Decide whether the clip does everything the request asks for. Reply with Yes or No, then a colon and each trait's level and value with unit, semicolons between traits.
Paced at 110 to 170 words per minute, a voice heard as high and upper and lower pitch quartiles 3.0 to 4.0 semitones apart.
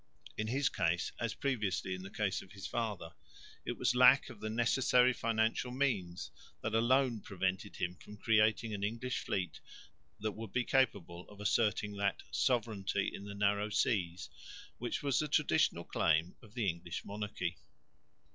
No: average, 160 wpm; low, 105 Hz; average, 3.7 semitones